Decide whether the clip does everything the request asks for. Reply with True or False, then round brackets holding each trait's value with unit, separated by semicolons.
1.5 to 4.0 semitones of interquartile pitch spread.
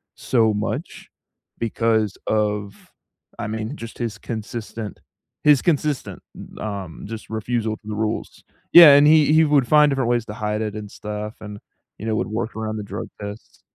True (2.5 semitones)